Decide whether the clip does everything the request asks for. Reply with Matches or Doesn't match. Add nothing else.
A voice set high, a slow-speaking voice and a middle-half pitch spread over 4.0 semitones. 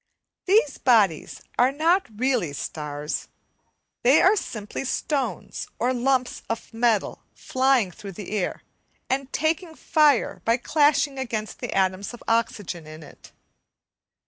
Matches